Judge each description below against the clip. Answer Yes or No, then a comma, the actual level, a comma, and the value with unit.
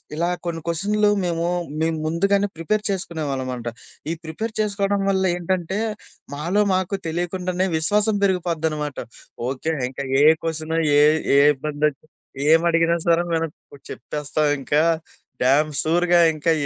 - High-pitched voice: No, medium, 165 Hz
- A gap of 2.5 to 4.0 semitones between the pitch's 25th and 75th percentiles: Yes, average, 3.3 semitones